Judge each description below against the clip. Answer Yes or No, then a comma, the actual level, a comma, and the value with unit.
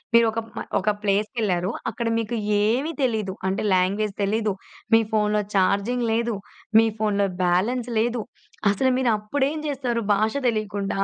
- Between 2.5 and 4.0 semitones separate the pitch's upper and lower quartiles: Yes, average, 2.8 semitones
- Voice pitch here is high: Yes, high, 215 Hz